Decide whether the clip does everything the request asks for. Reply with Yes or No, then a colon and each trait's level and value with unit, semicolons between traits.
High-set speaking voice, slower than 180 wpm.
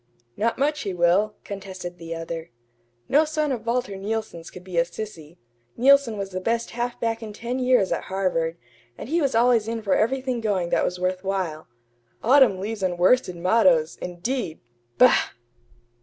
Yes: high, 205 Hz; average, 170 wpm